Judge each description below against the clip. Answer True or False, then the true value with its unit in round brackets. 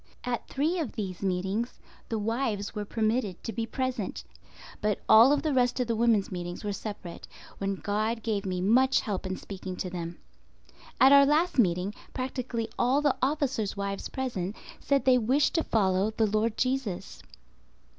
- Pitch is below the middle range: False (220 Hz)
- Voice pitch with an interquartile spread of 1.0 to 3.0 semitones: False (4.6 semitones)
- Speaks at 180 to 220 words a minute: False (165 wpm)